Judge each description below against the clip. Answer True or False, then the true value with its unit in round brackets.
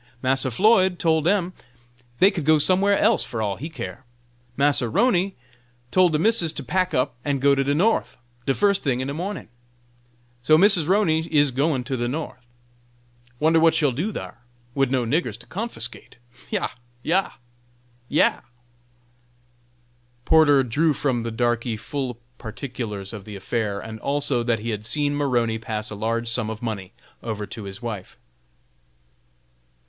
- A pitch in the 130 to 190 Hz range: True (135 Hz)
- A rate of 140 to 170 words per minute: True (160 wpm)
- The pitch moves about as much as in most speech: False (5.8 semitones)